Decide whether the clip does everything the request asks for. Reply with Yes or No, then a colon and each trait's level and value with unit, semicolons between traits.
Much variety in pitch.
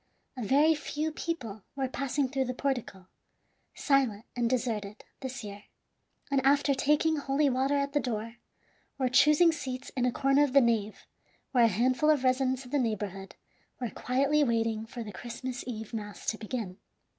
No: average, 3.5 semitones